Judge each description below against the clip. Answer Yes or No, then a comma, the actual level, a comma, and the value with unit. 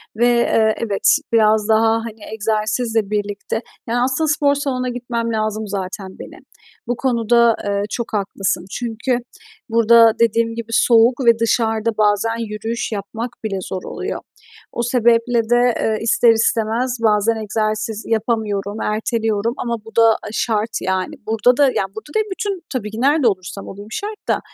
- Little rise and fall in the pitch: Yes, narrow, 1.9 semitones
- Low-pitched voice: No, high, 225 Hz